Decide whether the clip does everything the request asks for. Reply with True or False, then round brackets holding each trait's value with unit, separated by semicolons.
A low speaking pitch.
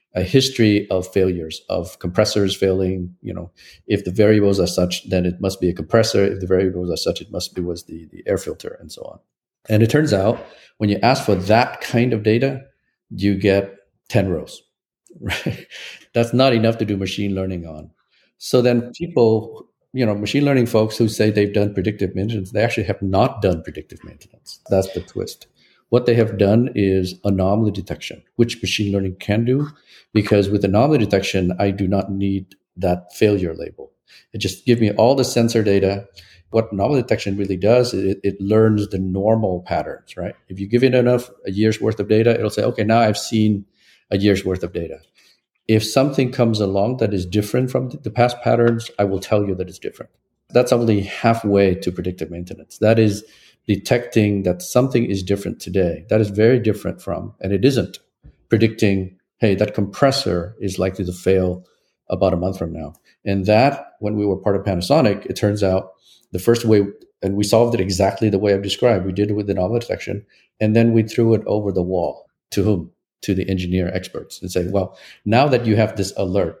True (100 Hz)